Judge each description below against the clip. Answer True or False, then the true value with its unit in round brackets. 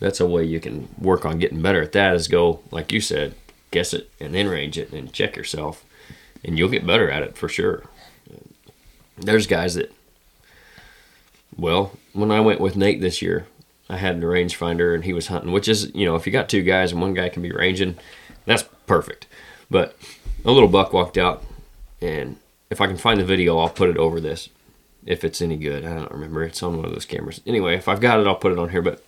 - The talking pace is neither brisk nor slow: False (235 wpm)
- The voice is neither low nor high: False (90 Hz)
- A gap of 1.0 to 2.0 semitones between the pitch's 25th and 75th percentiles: False (2.8 semitones)